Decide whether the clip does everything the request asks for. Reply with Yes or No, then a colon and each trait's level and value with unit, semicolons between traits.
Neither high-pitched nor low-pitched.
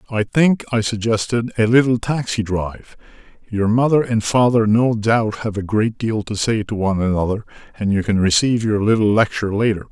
No: low, 110 Hz